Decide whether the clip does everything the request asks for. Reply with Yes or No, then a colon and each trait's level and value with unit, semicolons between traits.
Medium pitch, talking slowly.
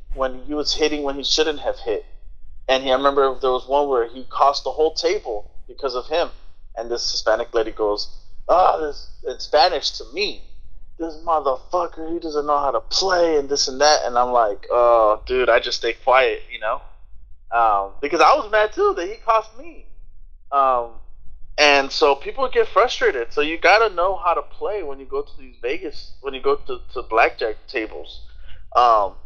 No: medium, 150 Hz; average, 200 wpm